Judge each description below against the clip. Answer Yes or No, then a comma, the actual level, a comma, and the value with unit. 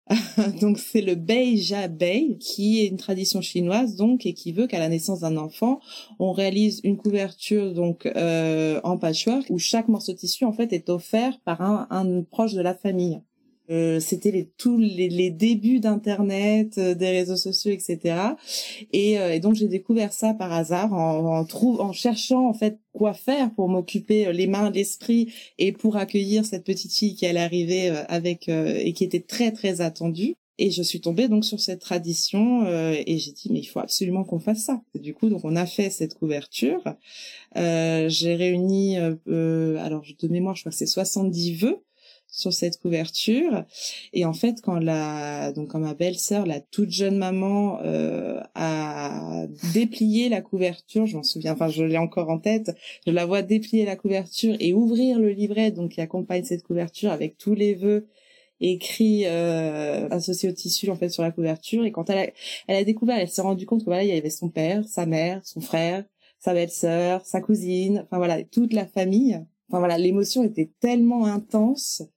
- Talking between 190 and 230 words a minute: Yes, average, 195 wpm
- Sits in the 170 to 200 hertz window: Yes, high, 190 Hz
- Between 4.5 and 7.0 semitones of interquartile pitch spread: No, average, 4.0 semitones